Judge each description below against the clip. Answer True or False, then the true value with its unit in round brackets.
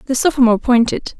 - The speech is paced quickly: False (150 wpm)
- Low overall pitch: False (250 Hz)